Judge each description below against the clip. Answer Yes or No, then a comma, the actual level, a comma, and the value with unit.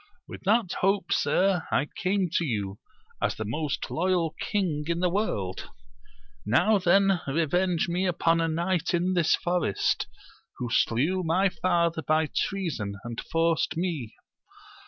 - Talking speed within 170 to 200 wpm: No, average, 145 wpm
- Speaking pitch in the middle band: Yes, medium, 170 Hz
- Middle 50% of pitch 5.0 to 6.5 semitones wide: No, average, 3.5 semitones